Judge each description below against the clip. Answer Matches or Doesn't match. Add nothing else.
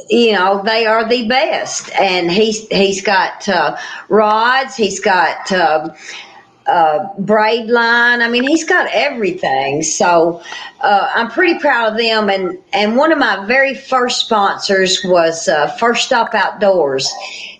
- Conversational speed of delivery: Matches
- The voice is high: Matches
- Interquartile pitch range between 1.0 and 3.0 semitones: Doesn't match